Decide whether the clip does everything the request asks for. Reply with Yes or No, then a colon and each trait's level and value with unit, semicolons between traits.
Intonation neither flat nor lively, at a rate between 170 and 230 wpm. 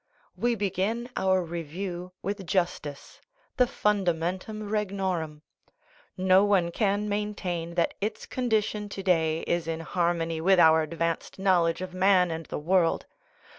No: average, 3.3 semitones; slow, 135 wpm